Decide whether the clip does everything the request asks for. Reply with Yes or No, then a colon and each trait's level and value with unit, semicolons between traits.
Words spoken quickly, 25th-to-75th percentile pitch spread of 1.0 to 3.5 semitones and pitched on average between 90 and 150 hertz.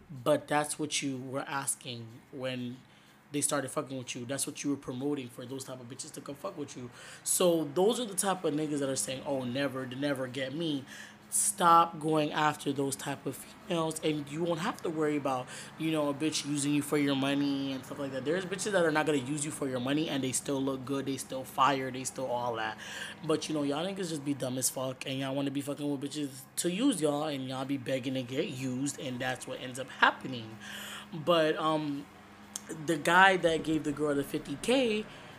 Yes: fast, 230 wpm; average, 2.9 semitones; medium, 140 Hz